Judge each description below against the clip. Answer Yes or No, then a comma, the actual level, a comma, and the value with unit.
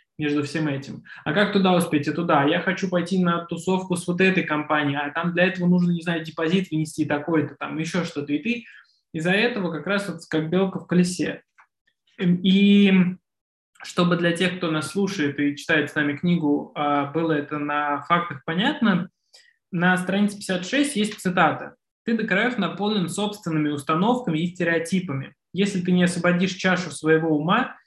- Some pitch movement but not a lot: Yes, average, 3.4 semitones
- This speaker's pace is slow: No, fast, 170 wpm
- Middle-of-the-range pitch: Yes, medium, 175 Hz